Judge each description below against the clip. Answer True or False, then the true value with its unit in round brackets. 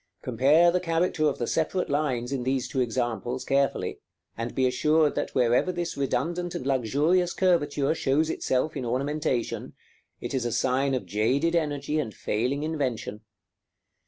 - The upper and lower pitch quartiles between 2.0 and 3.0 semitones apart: False (4.0 semitones)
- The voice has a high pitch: False (140 Hz)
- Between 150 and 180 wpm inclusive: True (155 wpm)